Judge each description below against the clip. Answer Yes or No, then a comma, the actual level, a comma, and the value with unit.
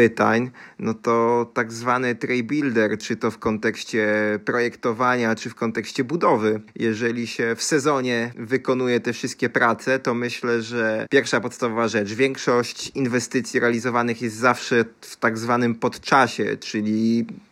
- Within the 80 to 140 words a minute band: Yes, average, 135 wpm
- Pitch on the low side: Yes, low, 120 Hz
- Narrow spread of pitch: Yes, narrow, 1.6 semitones